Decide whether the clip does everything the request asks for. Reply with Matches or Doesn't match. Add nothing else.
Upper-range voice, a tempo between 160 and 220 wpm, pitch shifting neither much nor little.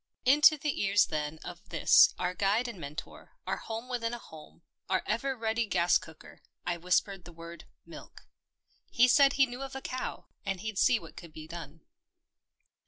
Doesn't match